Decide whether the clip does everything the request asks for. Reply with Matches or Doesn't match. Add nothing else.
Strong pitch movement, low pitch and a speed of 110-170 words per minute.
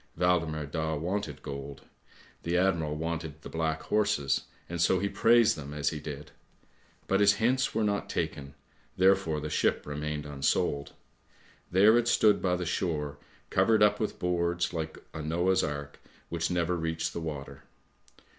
Doesn't match